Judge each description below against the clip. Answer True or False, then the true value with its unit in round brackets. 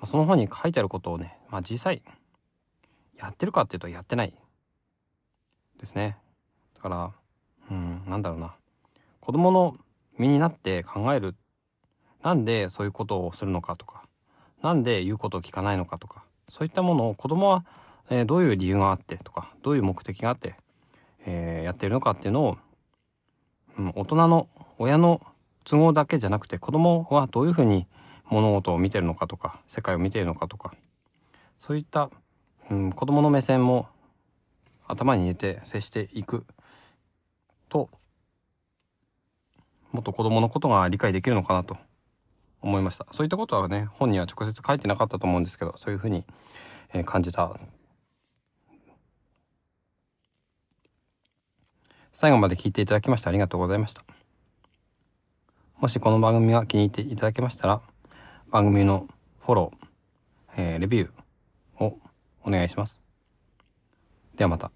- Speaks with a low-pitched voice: True (105 Hz)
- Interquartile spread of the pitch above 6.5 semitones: False (5.6 semitones)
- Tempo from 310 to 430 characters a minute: True (315 characters per minute)